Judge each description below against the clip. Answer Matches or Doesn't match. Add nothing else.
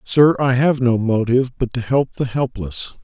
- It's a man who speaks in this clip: Matches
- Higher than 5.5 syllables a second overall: Doesn't match